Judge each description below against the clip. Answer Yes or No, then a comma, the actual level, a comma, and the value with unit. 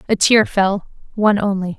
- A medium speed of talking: Yes, average, 170 wpm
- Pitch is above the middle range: Yes, high, 200 Hz